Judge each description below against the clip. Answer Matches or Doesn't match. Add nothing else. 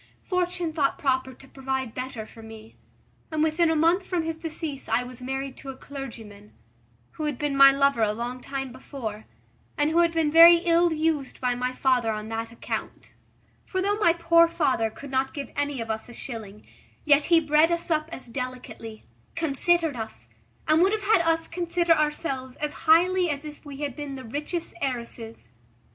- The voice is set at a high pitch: Matches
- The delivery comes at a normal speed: Matches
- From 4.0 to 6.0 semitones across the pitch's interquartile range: Matches